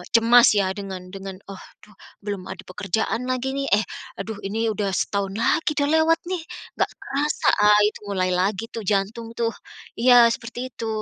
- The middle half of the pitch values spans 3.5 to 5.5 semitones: Yes, average, 3.8 semitones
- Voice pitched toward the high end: Yes, high, 220 Hz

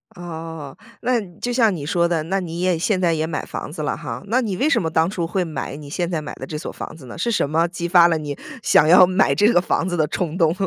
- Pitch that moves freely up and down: No, average, 2.9 semitones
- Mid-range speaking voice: Yes, medium, 170 Hz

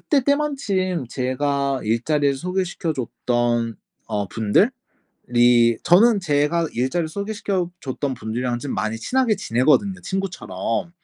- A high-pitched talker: No, medium, 145 Hz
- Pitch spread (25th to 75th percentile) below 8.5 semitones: Yes, wide, 7.9 semitones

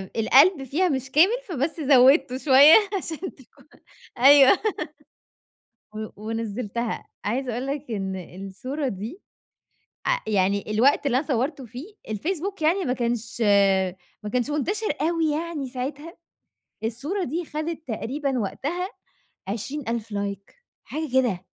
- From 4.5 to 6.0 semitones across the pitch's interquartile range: Yes, average, 5.2 semitones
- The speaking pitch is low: No, very high, 270 Hz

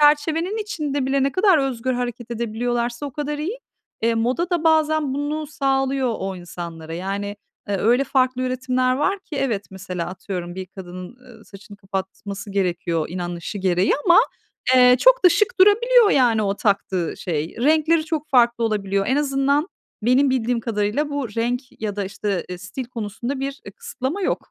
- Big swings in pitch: Yes, wide, 6.6 semitones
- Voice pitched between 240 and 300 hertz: Yes, high, 245 Hz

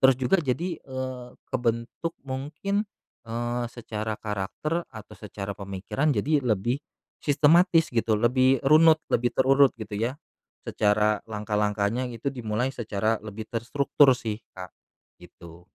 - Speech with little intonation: No, average, 4.3 semitones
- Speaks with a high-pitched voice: No, low, 120 Hz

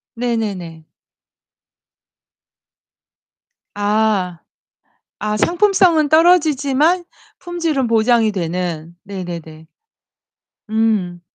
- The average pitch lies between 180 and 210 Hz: No, high, 220 Hz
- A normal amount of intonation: No, wide, 9.0 semitones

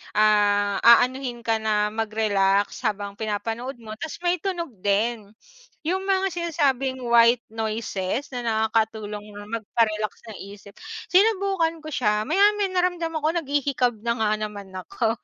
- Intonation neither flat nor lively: No, wide, 6.4 semitones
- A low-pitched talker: No, high, 230 Hz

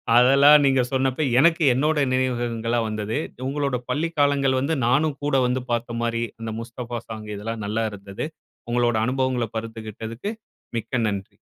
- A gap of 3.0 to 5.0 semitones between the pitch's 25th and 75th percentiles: Yes, average, 3.3 semitones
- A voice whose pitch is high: No, low, 120 Hz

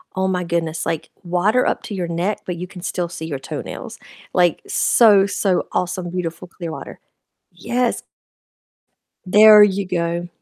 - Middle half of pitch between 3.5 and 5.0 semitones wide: No, narrow, 2.5 semitones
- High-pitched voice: No, medium, 180 Hz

